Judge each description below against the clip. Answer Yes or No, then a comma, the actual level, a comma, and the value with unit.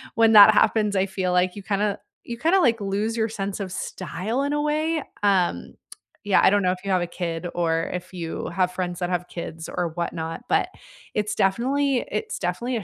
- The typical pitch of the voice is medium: No, high, 195 Hz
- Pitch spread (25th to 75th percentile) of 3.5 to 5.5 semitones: Yes, average, 3.9 semitones